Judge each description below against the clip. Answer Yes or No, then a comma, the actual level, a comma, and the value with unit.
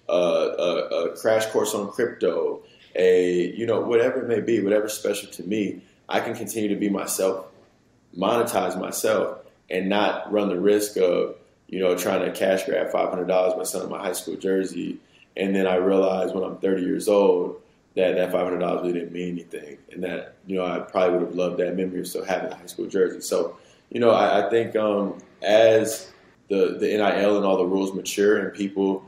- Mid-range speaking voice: No, low, 100 Hz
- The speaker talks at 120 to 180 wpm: No, average, 200 wpm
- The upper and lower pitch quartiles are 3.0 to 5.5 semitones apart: Yes, average, 3.7 semitones